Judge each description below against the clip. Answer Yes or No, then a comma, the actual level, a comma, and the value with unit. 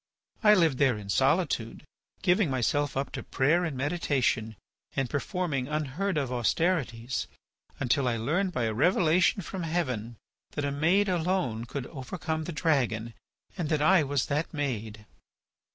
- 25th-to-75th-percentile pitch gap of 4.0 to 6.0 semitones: Yes, wide, 5.5 semitones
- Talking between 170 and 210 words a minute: No, average, 150 wpm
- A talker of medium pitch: Yes, medium, 145 Hz